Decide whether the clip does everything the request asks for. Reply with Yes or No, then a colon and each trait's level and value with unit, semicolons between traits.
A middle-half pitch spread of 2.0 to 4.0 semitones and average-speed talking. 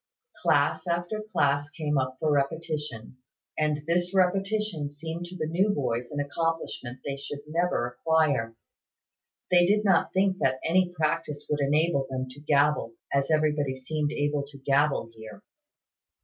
Yes: average, 3.5 semitones; average, 150 wpm